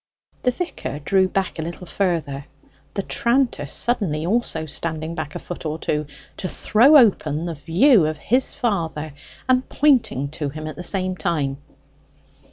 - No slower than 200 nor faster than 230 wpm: No, average, 160 wpm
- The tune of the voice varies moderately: No, wide, 6.2 semitones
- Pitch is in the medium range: Yes, medium, 170 Hz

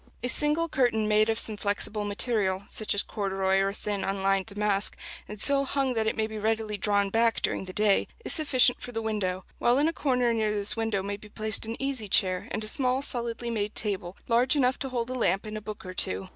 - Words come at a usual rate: No, fast, 230 wpm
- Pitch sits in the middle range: No, high, 215 Hz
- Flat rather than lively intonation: No, average, 3.2 semitones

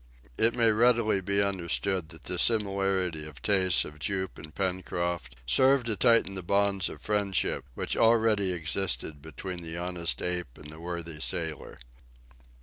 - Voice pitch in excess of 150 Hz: No, very low, 95 Hz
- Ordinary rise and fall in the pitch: Yes, average, 3.3 semitones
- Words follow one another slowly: No, average, 150 wpm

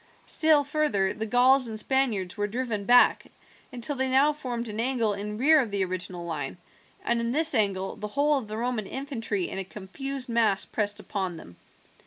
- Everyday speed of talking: Yes, average, 190 wpm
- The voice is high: Yes, high, 230 Hz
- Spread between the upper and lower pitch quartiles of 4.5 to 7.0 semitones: Yes, average, 4.8 semitones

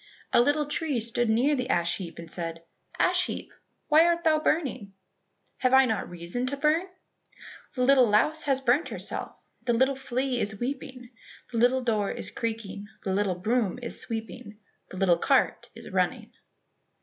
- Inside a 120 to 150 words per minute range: No, average, 170 wpm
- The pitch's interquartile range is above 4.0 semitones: Yes, average, 5.0 semitones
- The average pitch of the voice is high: Yes, high, 245 Hz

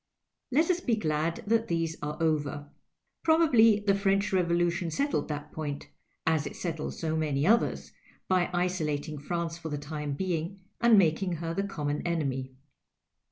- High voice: No, medium, 170 Hz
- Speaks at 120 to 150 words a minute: No, average, 160 wpm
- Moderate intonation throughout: Yes, average, 4.5 semitones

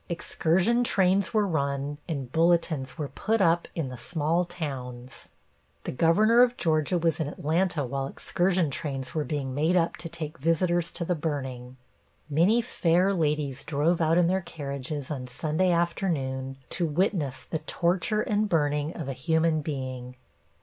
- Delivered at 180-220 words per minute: No, average, 155 wpm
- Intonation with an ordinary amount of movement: Yes, average, 3.8 semitones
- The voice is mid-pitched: Yes, medium, 160 Hz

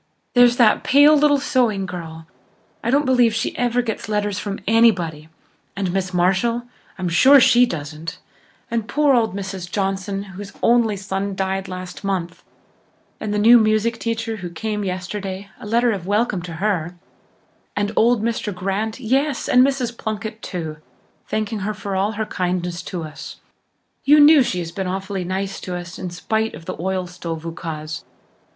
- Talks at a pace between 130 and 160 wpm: No, average, 170 wpm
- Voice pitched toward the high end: Yes, high, 200 Hz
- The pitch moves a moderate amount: Yes, average, 4.0 semitones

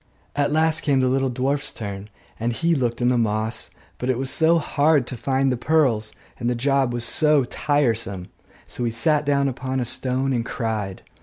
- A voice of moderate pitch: No, low, 130 Hz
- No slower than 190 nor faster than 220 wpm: Yes, average, 200 wpm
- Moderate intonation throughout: Yes, average, 3.4 semitones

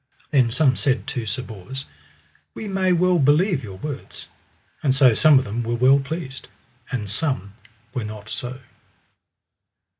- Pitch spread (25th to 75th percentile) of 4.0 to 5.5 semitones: Yes, average, 4.5 semitones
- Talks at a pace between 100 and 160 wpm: Yes, average, 150 wpm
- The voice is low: Yes, low, 130 Hz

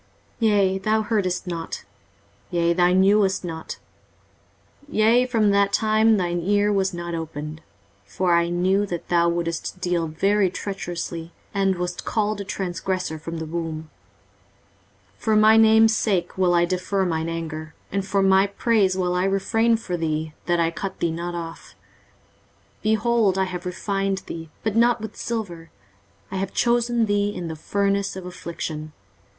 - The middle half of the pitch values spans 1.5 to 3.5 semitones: Yes, average, 3.2 semitones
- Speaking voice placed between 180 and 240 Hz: Yes, medium, 185 Hz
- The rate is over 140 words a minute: Yes, average, 165 wpm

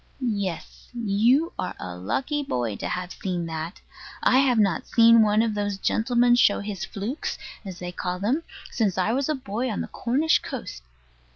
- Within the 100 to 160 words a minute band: No, average, 180 wpm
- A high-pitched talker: Yes, high, 210 Hz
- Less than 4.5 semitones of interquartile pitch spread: No, average, 5.1 semitones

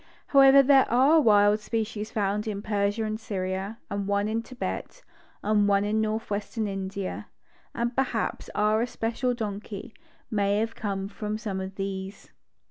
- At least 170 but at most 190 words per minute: No, average, 145 wpm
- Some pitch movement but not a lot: No, narrow, 2.1 semitones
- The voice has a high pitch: Yes, high, 210 Hz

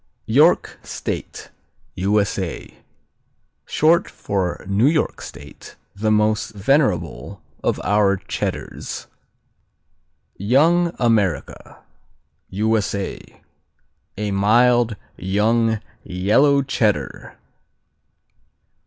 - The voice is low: Yes, low, 105 Hz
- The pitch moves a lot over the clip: No, average, 3.7 semitones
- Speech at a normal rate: No, slow, 70 wpm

